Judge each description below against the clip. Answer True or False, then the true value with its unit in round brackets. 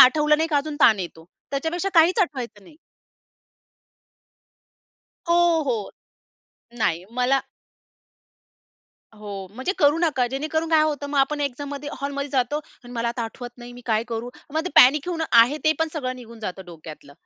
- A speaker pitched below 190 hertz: False (270 Hz)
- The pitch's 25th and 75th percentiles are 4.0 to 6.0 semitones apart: True (4.6 semitones)